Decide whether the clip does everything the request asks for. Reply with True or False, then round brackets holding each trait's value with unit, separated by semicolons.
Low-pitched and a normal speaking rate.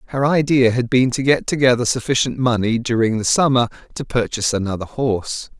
True (120 Hz; 170 wpm)